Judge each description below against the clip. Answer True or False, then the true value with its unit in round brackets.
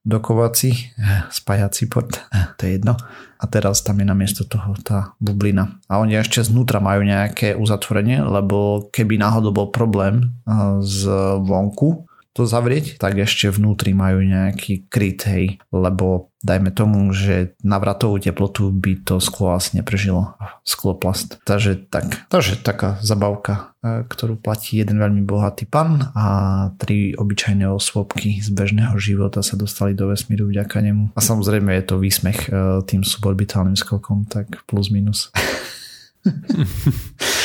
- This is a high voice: False (100 Hz)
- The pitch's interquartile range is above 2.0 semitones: False (1.7 semitones)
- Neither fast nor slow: True (135 wpm)